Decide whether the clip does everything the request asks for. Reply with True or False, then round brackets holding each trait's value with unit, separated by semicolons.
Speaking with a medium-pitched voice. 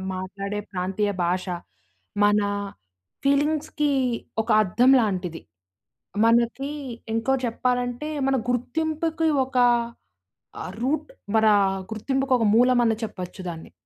False (240 Hz)